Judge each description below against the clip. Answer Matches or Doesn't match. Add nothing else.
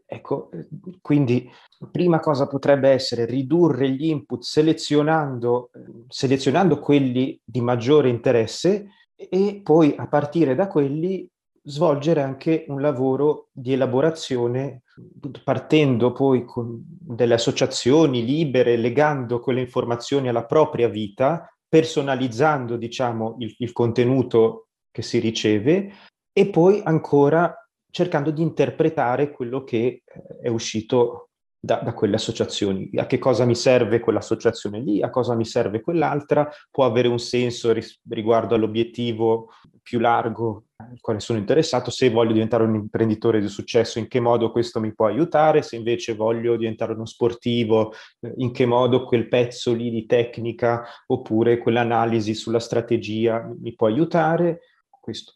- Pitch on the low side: Matches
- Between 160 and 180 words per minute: Doesn't match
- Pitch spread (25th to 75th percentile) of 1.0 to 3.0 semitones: Doesn't match